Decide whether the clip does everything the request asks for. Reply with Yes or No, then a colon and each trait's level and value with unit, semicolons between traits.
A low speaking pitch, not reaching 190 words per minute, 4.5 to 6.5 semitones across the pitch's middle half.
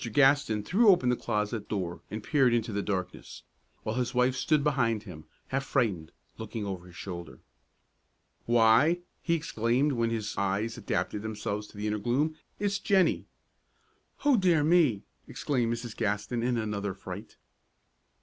Yes: low, 115 Hz; average, 155 wpm; average, 4.9 semitones